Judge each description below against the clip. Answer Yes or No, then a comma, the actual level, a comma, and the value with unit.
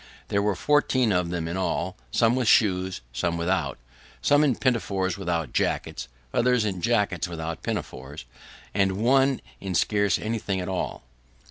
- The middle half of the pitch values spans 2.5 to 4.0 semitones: No, average, 4.8 semitones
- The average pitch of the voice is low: Yes, very low, 95 Hz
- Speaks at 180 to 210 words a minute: No, average, 150 wpm